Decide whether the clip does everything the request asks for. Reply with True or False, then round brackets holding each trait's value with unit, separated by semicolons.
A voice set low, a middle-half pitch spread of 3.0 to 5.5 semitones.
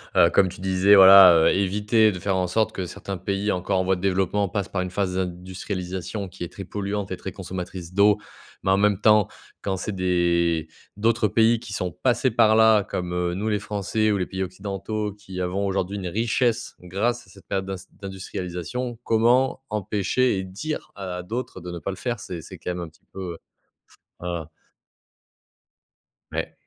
False (95 Hz; 2.6 semitones)